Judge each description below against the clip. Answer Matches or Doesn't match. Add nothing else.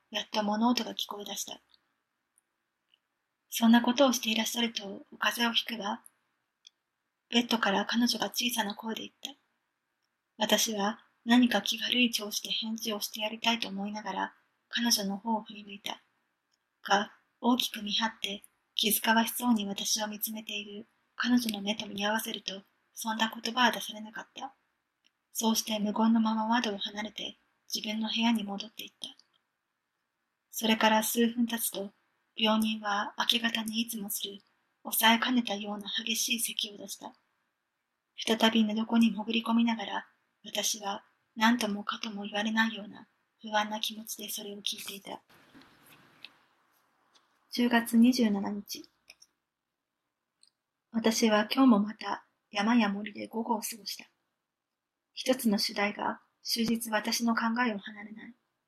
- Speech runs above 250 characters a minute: Matches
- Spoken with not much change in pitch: Matches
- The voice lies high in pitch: Matches